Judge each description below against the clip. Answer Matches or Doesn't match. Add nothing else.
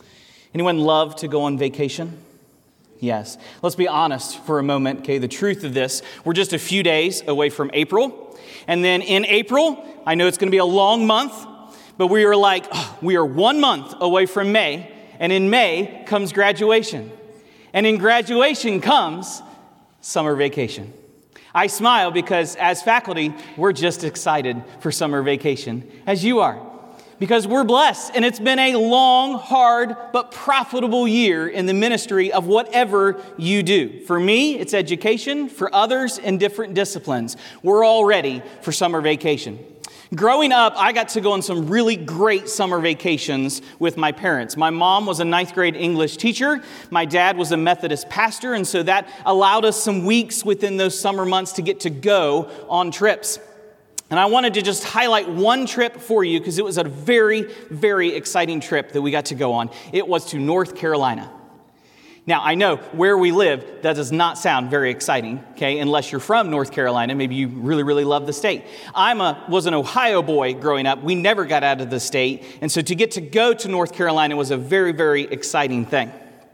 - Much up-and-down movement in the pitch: Matches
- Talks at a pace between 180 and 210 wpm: Matches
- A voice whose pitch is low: Doesn't match